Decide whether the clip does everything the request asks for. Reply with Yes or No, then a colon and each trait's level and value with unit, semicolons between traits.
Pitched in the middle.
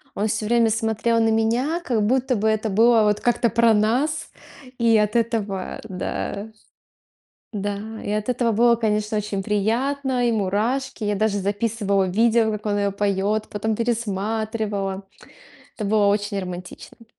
No: high, 215 Hz